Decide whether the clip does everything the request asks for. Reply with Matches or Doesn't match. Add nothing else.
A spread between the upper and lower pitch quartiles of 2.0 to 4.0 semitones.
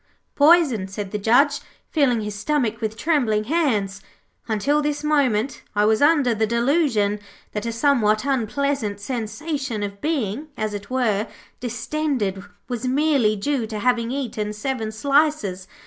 Doesn't match